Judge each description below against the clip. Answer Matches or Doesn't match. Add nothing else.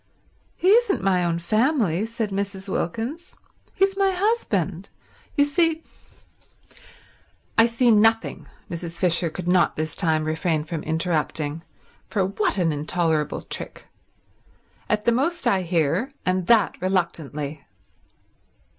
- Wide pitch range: Matches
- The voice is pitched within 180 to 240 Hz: Matches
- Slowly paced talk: Matches